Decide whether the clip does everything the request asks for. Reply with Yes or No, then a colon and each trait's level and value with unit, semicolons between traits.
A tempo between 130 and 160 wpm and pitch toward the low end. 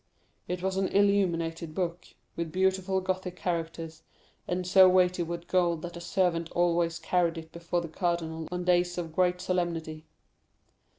No: average, 155 wpm; medium, 175 Hz